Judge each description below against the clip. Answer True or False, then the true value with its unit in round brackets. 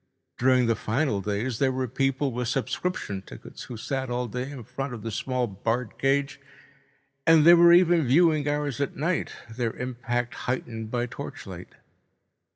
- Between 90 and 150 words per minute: False (160 wpm)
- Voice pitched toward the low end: True (130 Hz)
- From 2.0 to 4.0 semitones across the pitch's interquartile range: True (3.1 semitones)